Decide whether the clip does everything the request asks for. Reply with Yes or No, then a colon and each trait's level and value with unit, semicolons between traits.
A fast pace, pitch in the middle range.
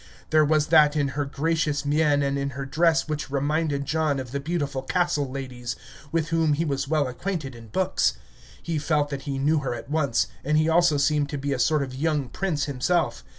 Yes: fast, 210 wpm; medium, 145 Hz